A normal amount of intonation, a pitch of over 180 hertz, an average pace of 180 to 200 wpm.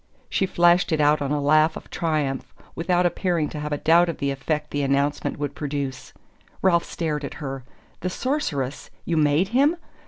No: average, 3.2 semitones; medium, 150 Hz; average, 185 wpm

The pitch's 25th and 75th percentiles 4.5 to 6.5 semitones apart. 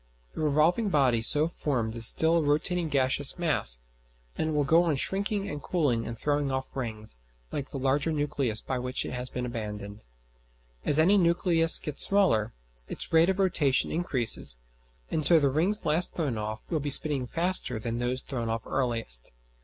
Yes: average, 5.2 semitones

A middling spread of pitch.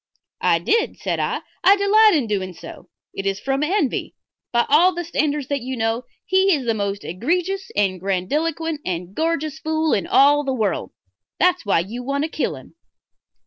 No: wide, 8.0 semitones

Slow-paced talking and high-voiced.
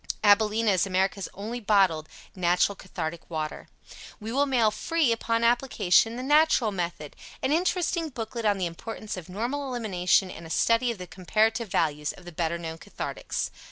No: average, 165 wpm; high, 210 Hz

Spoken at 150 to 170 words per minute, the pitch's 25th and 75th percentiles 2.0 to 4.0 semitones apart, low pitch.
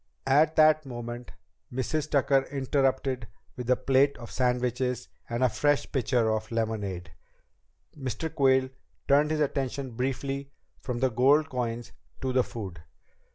No: slow, 135 wpm; average, 2.7 semitones; low, 130 Hz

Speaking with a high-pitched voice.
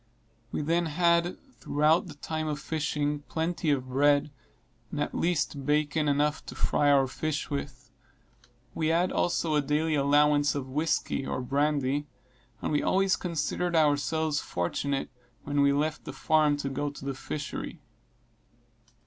No: medium, 150 Hz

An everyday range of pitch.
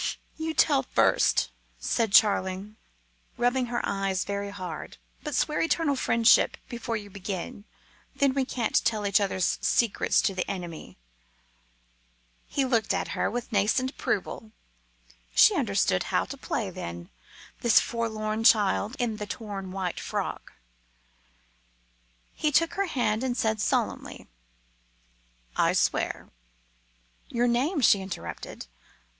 Yes: average, 3.9 semitones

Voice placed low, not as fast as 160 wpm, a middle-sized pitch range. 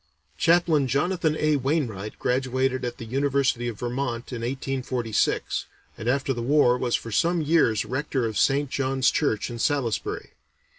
Yes: low, 130 Hz; average, 150 wpm; average, 3.1 semitones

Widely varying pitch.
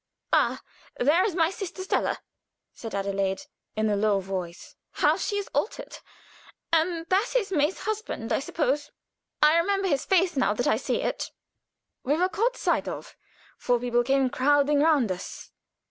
Yes: wide, 7.8 semitones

